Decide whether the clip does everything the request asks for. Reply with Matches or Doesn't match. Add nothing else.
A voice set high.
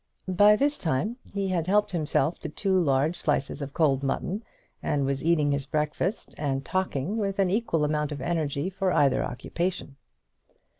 Doesn't match